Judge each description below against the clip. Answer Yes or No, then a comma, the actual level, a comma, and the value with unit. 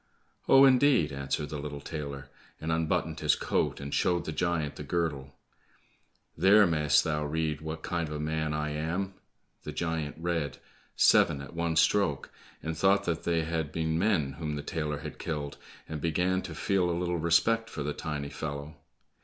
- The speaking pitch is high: No, very low, 80 Hz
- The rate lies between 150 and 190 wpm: Yes, average, 180 wpm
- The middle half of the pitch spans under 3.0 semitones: Yes, narrow, 2.5 semitones